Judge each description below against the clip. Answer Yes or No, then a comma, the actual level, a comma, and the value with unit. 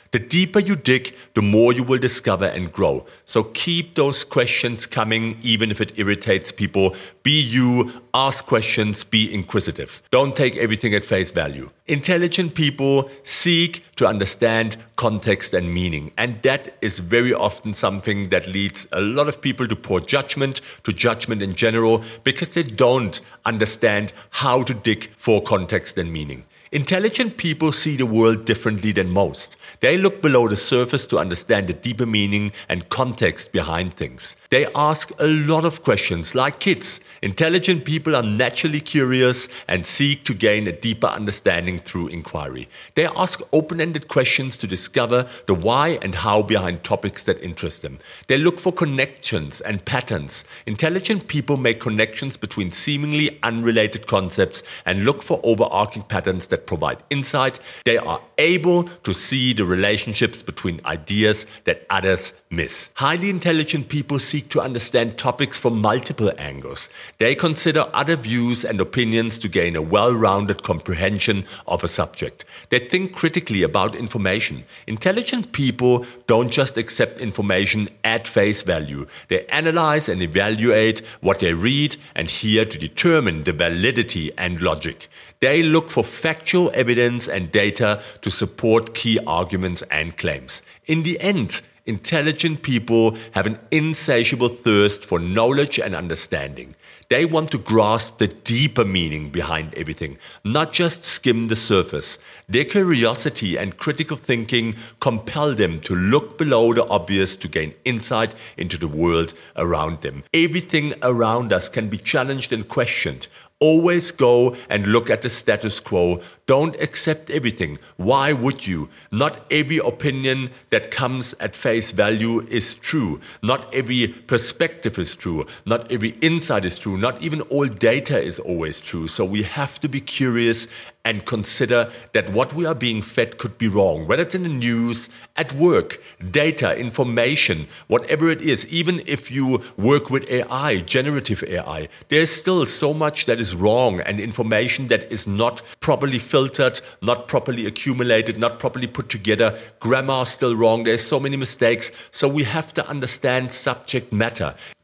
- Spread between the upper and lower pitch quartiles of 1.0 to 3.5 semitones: No, wide, 5.4 semitones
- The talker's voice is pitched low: Yes, low, 120 Hz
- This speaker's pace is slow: No, average, 155 wpm